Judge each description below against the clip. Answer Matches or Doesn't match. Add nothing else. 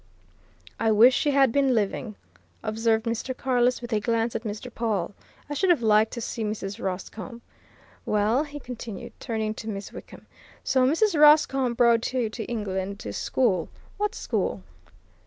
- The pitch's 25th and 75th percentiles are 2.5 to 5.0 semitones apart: Matches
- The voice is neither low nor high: Doesn't match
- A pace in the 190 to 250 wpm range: Doesn't match